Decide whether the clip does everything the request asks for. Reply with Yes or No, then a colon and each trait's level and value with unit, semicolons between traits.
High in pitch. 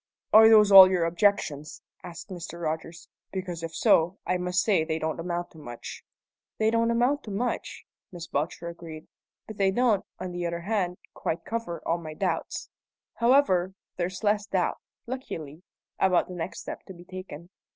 No: medium, 180 Hz